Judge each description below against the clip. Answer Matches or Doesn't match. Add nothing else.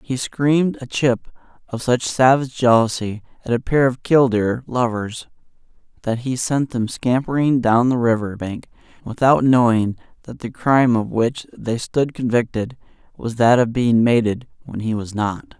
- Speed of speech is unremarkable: Matches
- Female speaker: Doesn't match